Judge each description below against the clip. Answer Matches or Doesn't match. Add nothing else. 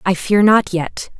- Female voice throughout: Matches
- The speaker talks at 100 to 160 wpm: Doesn't match